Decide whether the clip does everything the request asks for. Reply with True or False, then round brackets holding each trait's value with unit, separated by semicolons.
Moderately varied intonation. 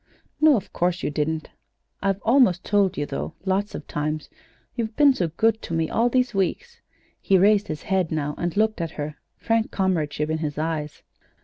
False (5.8 semitones)